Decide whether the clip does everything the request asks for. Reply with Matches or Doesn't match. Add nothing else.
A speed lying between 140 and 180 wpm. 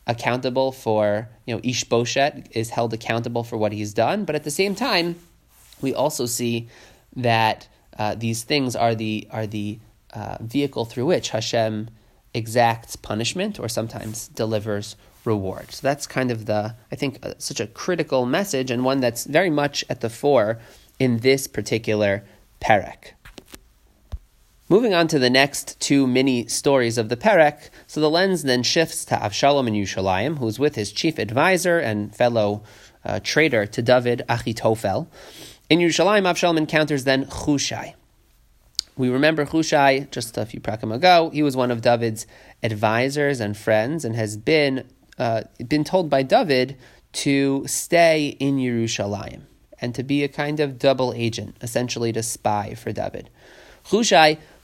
Matches